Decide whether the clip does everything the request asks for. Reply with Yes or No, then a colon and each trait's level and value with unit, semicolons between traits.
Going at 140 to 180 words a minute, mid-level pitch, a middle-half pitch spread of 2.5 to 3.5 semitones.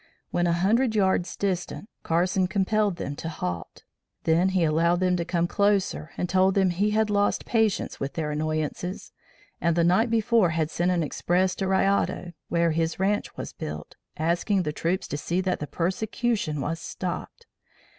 Yes: average, 175 wpm; medium, 180 Hz; average, 3.2 semitones